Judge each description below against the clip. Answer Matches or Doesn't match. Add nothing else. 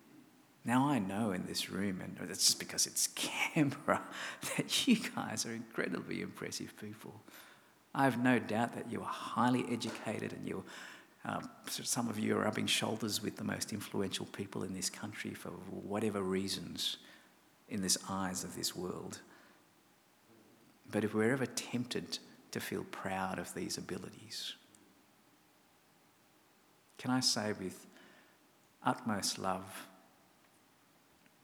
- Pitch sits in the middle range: Doesn't match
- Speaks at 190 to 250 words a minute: Doesn't match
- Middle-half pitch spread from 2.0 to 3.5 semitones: Doesn't match